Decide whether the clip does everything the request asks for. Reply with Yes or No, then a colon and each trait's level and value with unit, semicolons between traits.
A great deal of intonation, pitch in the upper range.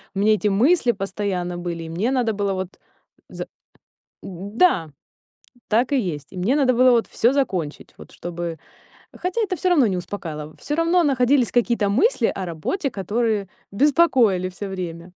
Yes: wide, 6.4 semitones; high, 205 Hz